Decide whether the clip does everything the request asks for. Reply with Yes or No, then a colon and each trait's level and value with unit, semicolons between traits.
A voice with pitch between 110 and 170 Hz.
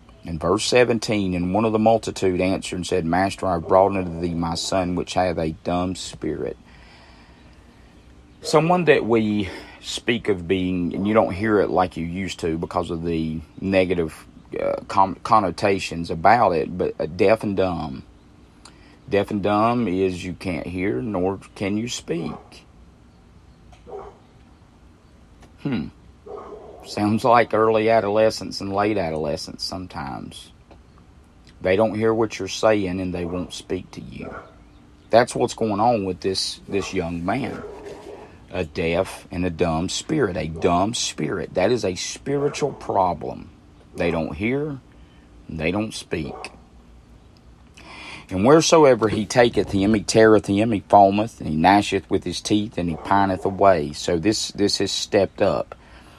No: very low, 95 Hz